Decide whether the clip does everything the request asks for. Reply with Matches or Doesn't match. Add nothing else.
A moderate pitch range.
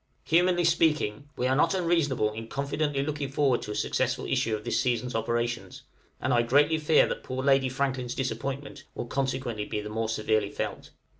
Matches